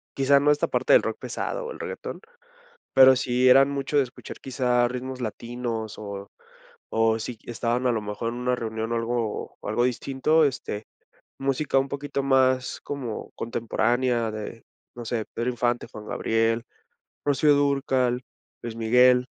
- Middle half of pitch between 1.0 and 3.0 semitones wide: Yes, average, 2.7 semitones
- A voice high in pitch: No, low, 125 Hz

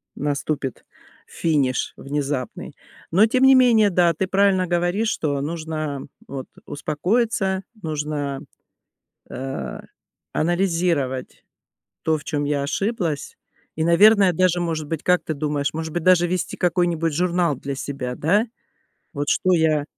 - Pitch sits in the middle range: Yes, medium, 160 Hz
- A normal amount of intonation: Yes, average, 4.0 semitones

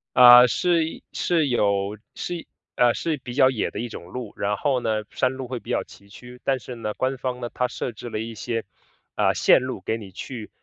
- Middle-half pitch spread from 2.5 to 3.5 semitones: Yes, average, 2.9 semitones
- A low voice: Yes, low, 125 Hz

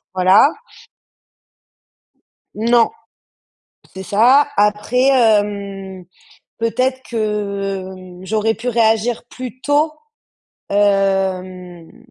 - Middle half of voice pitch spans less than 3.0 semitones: No, average, 3.3 semitones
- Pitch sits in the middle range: No, high, 210 Hz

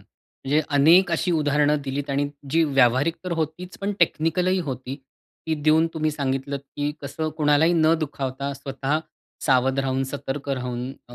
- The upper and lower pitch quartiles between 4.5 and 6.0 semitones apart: No, average, 2.8 semitones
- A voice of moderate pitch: Yes, medium, 145 Hz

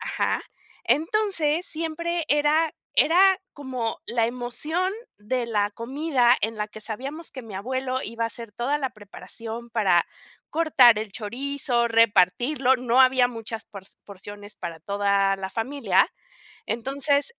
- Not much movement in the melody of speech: No, average, 4.8 semitones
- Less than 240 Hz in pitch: No, high, 245 Hz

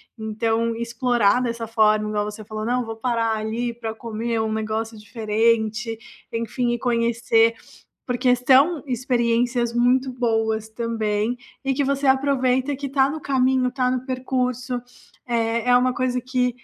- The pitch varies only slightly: Yes, narrow, 2.1 semitones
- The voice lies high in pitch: Yes, high, 235 Hz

